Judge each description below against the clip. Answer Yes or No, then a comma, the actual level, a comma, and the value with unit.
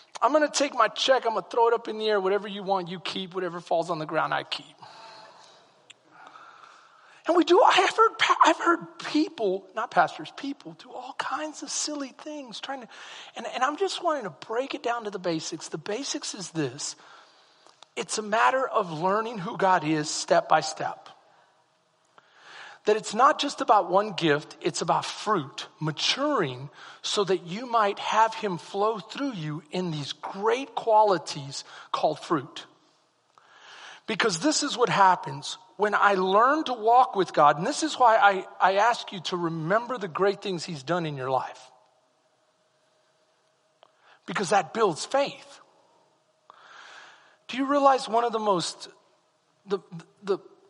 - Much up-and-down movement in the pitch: Yes, wide, 6.9 semitones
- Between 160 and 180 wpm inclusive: Yes, average, 170 wpm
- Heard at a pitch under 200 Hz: No, high, 205 Hz